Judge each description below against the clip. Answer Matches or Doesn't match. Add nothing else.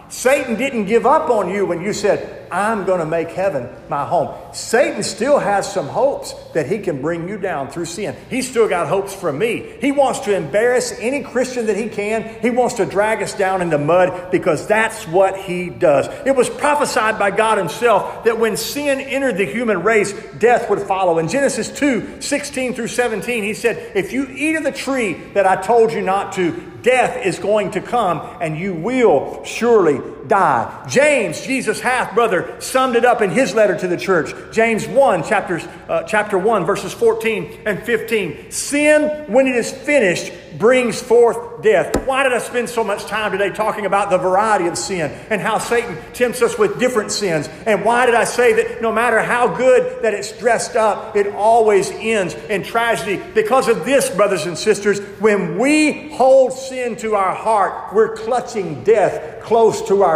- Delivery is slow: Doesn't match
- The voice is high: Matches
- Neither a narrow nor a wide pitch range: Matches